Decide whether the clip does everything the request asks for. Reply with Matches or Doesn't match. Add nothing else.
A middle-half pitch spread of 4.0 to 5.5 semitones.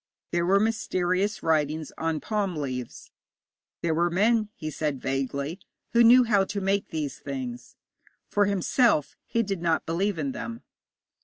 Matches